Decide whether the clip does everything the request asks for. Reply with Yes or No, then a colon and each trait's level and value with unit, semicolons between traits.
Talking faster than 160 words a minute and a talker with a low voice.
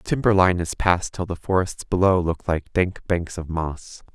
Yes: fast, 205 wpm; very low, 90 Hz